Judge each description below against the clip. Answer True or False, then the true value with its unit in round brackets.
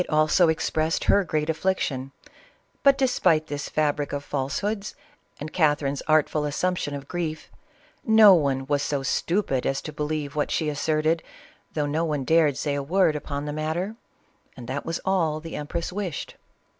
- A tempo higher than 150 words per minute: True (170 wpm)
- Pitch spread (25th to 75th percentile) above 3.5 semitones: False (2.6 semitones)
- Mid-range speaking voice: True (155 Hz)